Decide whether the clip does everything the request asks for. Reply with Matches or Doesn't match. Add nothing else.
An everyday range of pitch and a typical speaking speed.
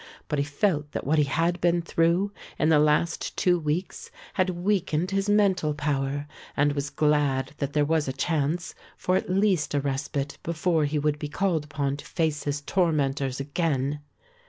Matches